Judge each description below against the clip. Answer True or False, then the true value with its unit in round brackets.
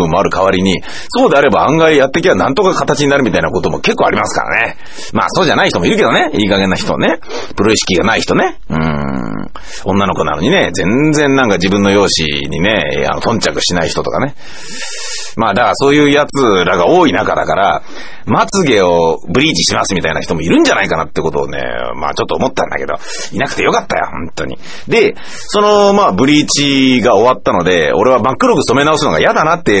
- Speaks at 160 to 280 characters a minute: False (425 characters per minute)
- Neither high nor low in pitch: False (120 Hz)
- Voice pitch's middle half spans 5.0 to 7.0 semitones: False (8.4 semitones)